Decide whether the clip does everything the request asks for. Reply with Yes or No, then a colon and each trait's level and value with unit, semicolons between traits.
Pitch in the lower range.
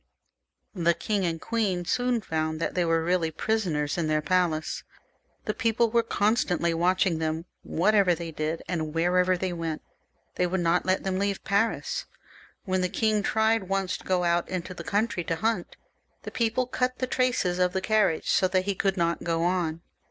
No: medium, 185 Hz